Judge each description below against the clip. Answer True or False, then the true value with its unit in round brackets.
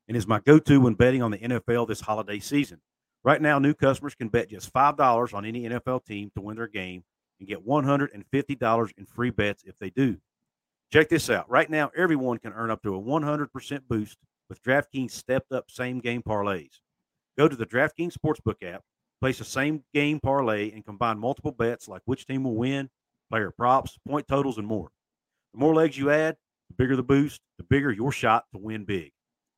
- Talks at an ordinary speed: False (215 wpm)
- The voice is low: True (120 Hz)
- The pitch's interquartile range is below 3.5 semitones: False (4.6 semitones)